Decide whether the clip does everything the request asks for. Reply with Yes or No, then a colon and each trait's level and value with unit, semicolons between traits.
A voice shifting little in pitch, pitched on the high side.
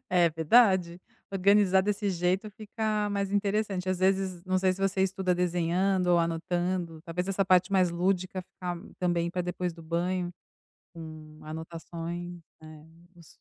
No: narrow, 2.1 semitones; medium, 180 Hz